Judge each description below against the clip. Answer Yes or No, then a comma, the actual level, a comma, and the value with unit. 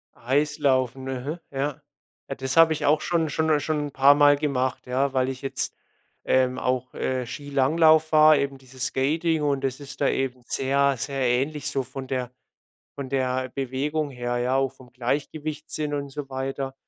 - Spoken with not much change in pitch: Yes, narrow, 2.2 semitones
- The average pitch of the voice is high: No, low, 135 Hz